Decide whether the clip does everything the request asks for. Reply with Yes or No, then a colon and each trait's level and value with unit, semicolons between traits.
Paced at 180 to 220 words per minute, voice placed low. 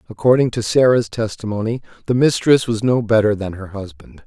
No: average, 170 wpm; low, 110 Hz